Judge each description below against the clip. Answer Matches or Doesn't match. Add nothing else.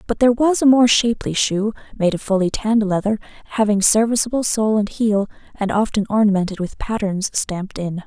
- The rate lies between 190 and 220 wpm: Doesn't match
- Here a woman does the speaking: Matches